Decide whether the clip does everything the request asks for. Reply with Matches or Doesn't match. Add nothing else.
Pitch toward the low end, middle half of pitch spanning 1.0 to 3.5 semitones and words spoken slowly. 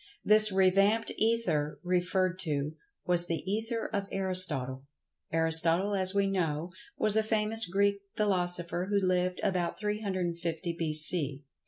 Doesn't match